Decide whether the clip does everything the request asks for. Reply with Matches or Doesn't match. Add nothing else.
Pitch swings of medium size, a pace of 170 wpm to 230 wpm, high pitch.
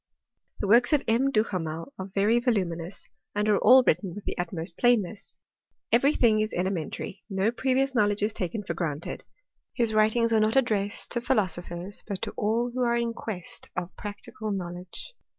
Matches